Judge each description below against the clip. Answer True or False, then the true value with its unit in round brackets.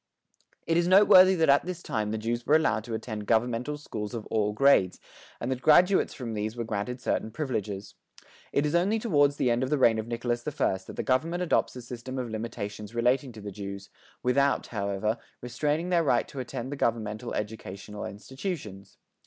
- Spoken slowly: False (195 wpm)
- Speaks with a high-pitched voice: False (120 Hz)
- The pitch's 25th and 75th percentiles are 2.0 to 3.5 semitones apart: False (5.0 semitones)